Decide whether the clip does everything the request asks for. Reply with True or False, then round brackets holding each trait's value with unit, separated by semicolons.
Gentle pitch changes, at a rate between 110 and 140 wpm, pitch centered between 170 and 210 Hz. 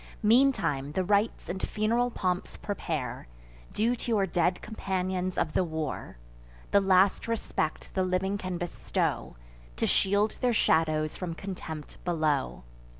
False (3.9 semitones; 135 wpm; 185 Hz)